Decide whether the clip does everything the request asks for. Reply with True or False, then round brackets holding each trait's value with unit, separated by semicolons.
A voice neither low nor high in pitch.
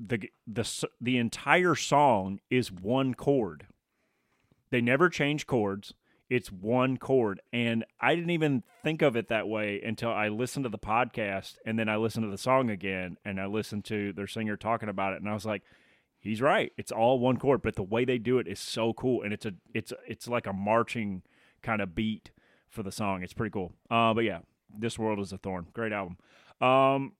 False (115 Hz)